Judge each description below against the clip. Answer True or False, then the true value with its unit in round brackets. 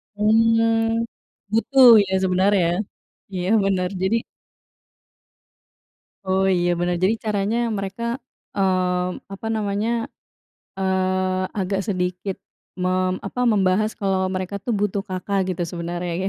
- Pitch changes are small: True (2.2 semitones)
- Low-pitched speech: False (190 Hz)